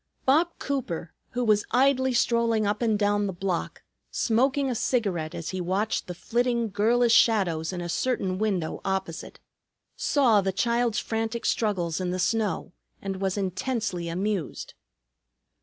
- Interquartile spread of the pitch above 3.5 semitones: Yes, average, 4.2 semitones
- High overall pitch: Yes, high, 210 Hz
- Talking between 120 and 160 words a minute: Yes, average, 145 wpm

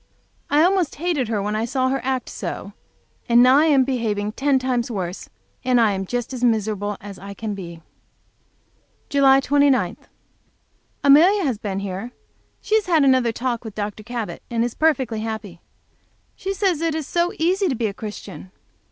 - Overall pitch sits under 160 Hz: No, high, 245 Hz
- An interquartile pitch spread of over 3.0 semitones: Yes, average, 5.1 semitones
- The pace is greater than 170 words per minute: Yes, average, 180 wpm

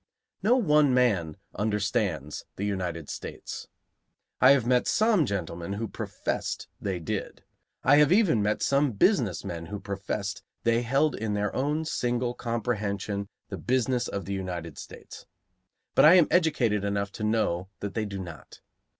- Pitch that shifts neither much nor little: Yes, average, 4.8 semitones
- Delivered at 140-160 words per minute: Yes, average, 155 wpm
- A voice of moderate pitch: No, low, 105 Hz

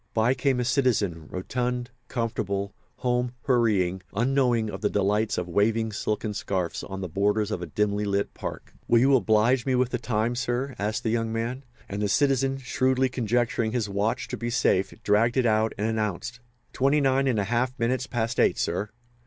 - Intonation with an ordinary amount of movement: Yes, average, 3.4 semitones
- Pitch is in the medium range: No, low, 115 Hz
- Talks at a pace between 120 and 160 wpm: No, average, 185 wpm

